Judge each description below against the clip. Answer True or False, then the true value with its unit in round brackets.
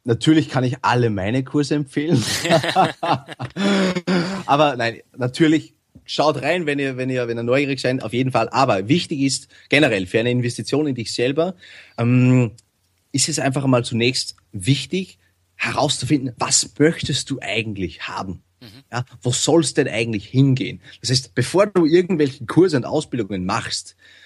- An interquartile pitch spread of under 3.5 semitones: False (4.3 semitones)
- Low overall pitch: True (130 Hz)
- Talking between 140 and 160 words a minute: True (150 wpm)